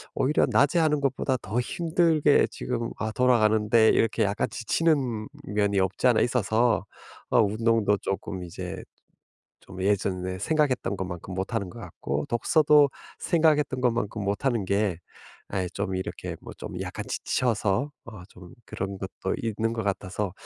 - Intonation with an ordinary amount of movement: Yes, average, 4.6 semitones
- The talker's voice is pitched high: No, low, 110 Hz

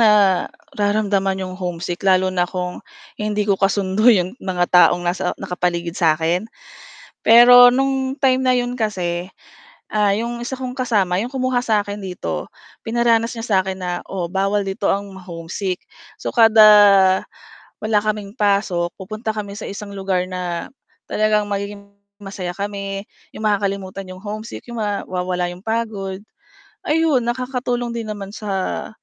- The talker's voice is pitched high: Yes, high, 200 Hz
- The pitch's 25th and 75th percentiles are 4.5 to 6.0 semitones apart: No, average, 3.2 semitones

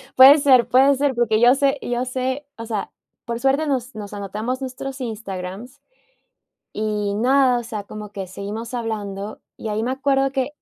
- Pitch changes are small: No, average, 3.8 semitones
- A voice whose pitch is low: No, high, 240 Hz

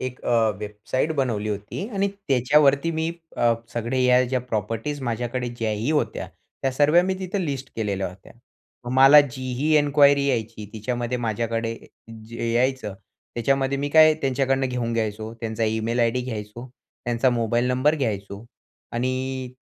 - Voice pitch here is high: No, low, 125 Hz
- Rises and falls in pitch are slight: No, average, 3.2 semitones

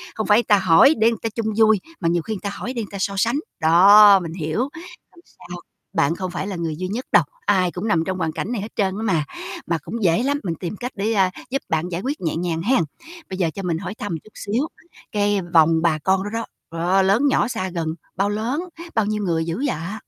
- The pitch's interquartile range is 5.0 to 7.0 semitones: No, average, 4.3 semitones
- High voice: Yes, high, 195 Hz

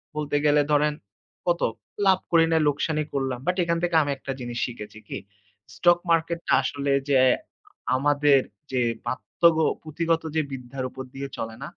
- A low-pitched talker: No, medium, 145 Hz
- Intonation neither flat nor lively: Yes, average, 3.5 semitones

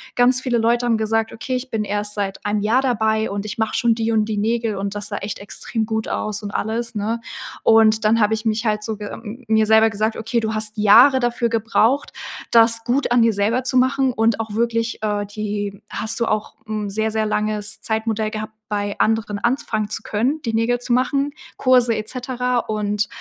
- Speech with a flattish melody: Yes, narrow, 1.9 semitones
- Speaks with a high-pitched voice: Yes, high, 220 Hz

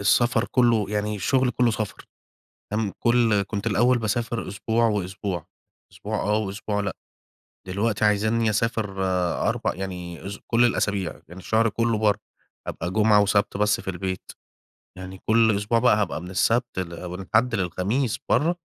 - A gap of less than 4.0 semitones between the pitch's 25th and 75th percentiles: Yes, average, 3.0 semitones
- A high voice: No, low, 105 Hz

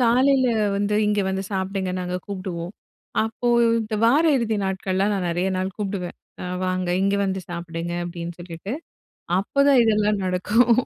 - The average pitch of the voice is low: No, high, 195 Hz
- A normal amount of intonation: Yes, average, 3.3 semitones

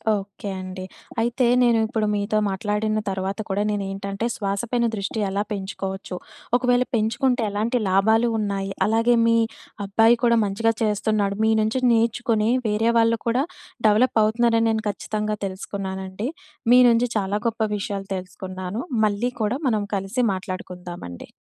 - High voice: Yes, high, 210 Hz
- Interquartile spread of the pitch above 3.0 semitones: No, average, 2.7 semitones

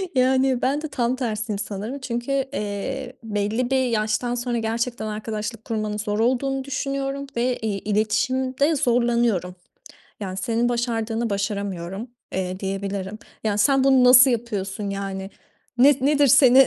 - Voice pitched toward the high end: Yes, high, 235 Hz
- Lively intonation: No, average, 3.8 semitones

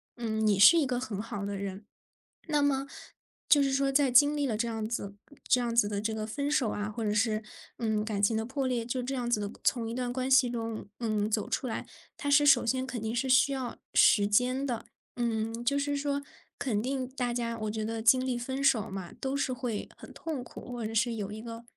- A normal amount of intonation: Yes, average, 3.3 semitones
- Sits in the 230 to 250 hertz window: Yes, high, 235 Hz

